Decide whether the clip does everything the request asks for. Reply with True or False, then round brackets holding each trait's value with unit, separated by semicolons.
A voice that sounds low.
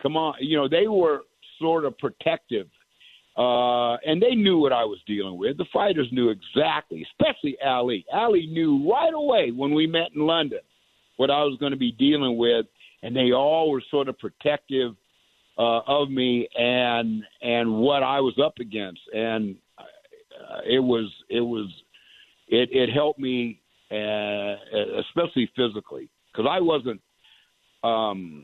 True (130 Hz)